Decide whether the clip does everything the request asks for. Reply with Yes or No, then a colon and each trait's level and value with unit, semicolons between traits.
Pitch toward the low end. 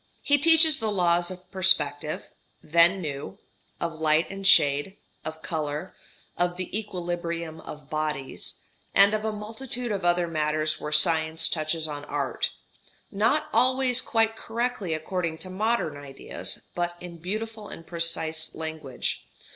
No: medium, 175 Hz